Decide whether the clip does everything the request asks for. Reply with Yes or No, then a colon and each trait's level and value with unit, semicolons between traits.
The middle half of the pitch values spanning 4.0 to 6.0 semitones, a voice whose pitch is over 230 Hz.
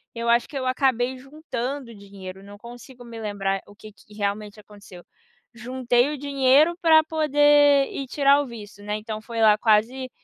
Yes: average, 4.6 semitones; high, 240 Hz